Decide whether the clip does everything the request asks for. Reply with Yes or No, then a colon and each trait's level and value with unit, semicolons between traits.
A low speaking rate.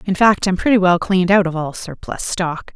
No: fast, 240 wpm